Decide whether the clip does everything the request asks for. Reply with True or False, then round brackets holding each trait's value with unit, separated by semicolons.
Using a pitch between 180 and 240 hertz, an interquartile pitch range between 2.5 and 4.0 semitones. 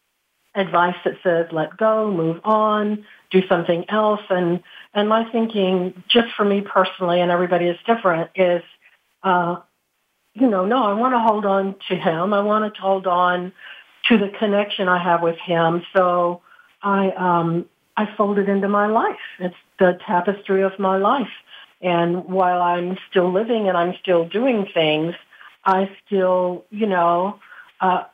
True (190 Hz; 2.9 semitones)